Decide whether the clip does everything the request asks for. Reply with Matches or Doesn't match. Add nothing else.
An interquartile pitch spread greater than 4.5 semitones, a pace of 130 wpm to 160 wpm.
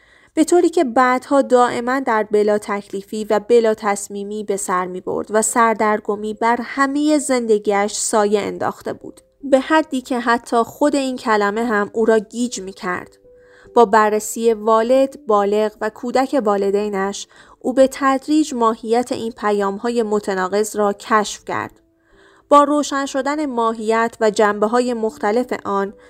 Doesn't match